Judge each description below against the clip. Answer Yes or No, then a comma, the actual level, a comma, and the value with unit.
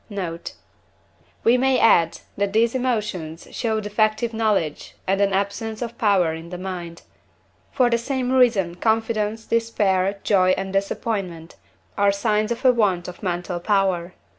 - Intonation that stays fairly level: No, average, 3.7 semitones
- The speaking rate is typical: Yes, average, 145 wpm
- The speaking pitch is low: No, high, 205 Hz